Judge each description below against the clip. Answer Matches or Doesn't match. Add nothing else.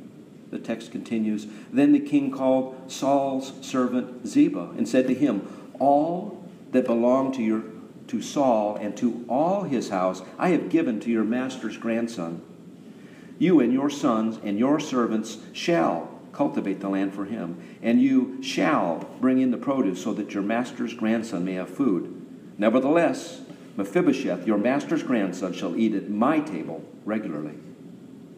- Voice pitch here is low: Matches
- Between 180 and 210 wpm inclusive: Doesn't match